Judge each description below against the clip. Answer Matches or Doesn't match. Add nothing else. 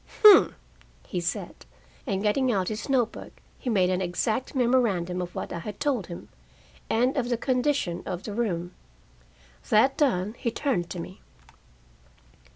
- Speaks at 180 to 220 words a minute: Doesn't match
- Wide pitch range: Matches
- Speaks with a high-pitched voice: Matches